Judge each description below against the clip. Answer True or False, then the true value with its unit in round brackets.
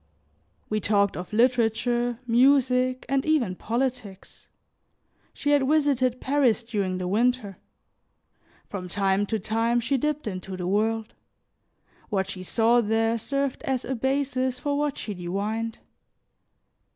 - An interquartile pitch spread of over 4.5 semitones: False (4.1 semitones)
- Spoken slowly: True (125 wpm)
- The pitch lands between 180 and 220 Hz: False (235 Hz)